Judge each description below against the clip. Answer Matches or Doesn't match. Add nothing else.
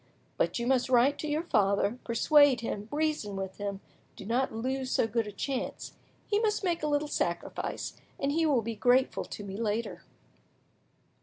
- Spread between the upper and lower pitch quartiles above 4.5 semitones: Matches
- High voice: Matches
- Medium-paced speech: Matches